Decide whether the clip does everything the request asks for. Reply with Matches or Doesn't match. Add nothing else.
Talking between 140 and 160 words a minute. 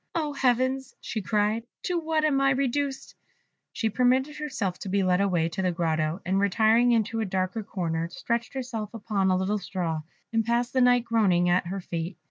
Doesn't match